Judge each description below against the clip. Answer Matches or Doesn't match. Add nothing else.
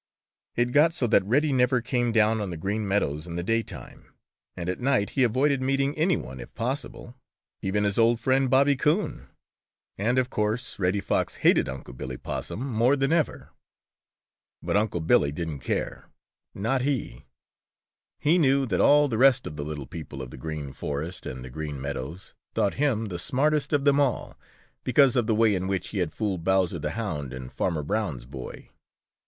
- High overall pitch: Doesn't match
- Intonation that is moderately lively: Doesn't match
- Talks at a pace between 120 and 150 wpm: Doesn't match